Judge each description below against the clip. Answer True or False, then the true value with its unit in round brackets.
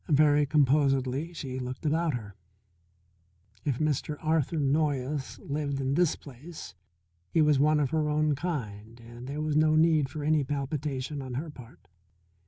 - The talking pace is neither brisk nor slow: True (155 wpm)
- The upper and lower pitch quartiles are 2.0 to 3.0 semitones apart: True (2.7 semitones)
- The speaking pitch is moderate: True (145 Hz)